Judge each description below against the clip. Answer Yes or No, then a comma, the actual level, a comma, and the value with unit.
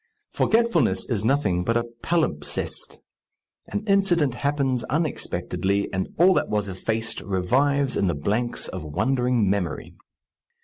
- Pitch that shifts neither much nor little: No, wide, 6.5 semitones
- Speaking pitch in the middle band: No, low, 120 Hz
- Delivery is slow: Yes, slow, 125 wpm